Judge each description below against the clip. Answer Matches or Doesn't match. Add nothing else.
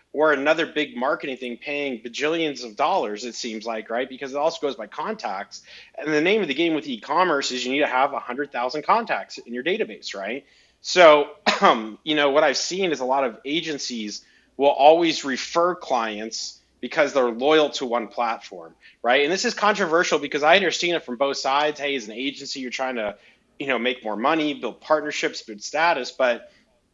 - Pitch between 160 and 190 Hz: Doesn't match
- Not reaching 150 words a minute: Doesn't match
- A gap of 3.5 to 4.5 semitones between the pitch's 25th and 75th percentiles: Matches